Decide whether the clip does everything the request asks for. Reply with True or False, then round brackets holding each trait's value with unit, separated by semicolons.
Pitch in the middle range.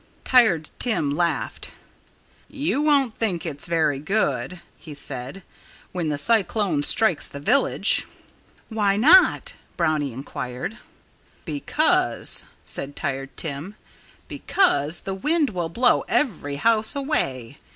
True (180 Hz)